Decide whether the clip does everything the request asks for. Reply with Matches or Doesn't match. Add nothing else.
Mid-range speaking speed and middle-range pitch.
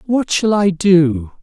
Matches